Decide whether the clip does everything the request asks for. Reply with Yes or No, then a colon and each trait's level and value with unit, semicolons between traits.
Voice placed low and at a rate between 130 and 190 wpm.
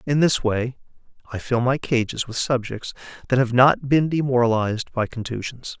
Yes: low, 125 Hz; average, 165 wpm